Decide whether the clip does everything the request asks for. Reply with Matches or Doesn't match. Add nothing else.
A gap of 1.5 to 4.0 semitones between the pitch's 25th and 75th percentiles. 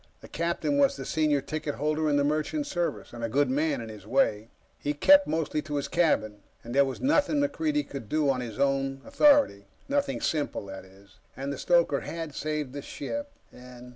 Doesn't match